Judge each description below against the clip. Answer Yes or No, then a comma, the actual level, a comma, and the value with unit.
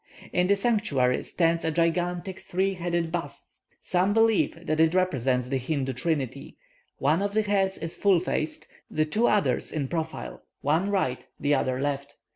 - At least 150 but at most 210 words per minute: Yes, average, 165 wpm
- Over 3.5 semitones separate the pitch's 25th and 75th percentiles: Yes, average, 5.0 semitones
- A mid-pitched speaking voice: Yes, medium, 165 Hz